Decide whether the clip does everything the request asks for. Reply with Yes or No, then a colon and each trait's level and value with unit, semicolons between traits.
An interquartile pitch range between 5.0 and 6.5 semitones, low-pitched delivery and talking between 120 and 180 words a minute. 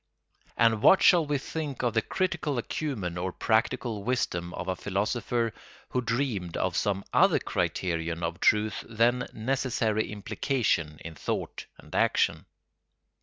Yes: average, 5.3 semitones; low, 110 Hz; slow, 135 wpm